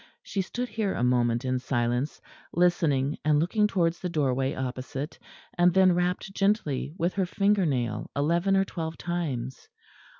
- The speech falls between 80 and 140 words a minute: No, average, 155 wpm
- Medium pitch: Yes, medium, 165 Hz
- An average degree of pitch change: No, wide, 5.9 semitones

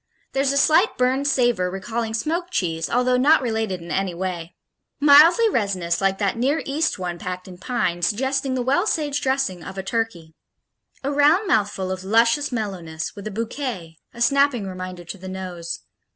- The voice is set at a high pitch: Yes, high, 225 Hz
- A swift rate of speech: No, average, 175 wpm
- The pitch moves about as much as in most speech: No, wide, 6.9 semitones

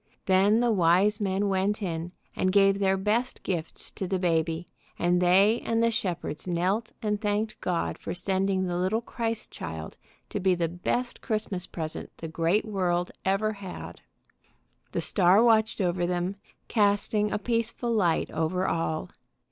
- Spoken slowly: No, average, 155 wpm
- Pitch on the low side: No, high, 190 Hz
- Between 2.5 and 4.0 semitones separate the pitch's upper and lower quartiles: Yes, average, 3.2 semitones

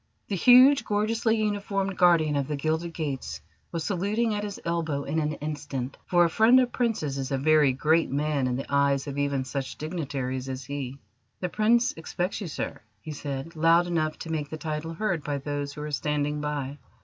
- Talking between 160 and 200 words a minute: Yes, average, 195 wpm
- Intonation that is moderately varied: Yes, average, 4.0 semitones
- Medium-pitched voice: Yes, medium, 155 Hz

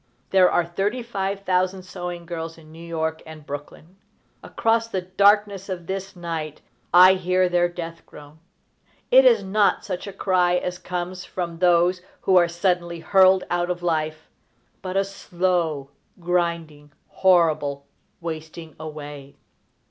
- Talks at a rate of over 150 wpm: No, average, 145 wpm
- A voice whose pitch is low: No, medium, 175 Hz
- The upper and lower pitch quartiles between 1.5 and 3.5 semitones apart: Yes, narrow, 2.4 semitones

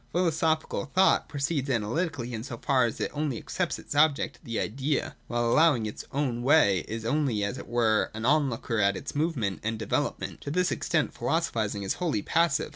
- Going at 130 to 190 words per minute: No, average, 200 wpm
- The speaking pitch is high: No, low, 135 Hz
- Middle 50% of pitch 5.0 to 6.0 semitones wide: Yes, wide, 5.6 semitones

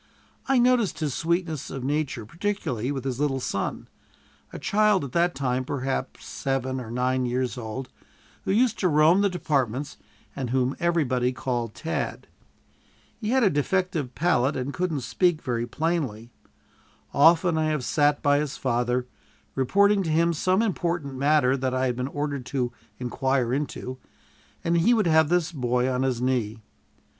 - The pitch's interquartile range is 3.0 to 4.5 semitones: No, average, 5.0 semitones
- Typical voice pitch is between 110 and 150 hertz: Yes, medium, 140 Hz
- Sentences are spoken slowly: No, average, 160 wpm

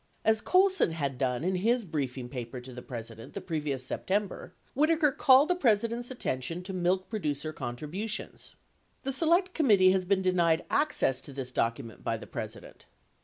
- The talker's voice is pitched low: No, medium, 180 Hz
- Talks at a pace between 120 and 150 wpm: No, average, 170 wpm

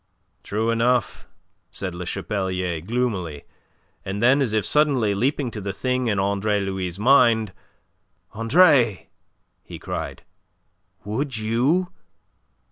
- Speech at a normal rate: No, slow, 115 wpm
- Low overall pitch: Yes, low, 110 Hz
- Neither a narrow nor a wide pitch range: Yes, average, 4.3 semitones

